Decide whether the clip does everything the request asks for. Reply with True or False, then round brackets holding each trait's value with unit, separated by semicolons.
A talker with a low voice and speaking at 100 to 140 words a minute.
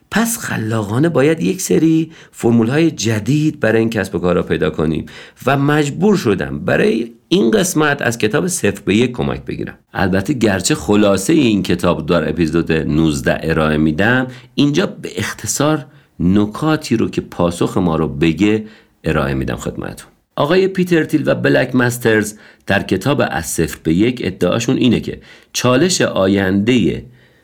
False (115 Hz; 150 wpm)